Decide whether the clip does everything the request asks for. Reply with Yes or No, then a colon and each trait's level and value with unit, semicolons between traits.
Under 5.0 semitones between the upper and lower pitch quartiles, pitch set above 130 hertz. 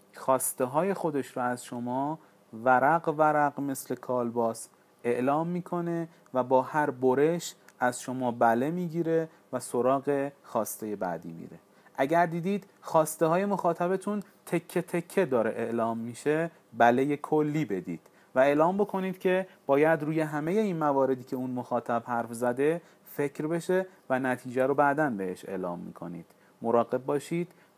No: average, 5.3 semitones; medium, 140 Hz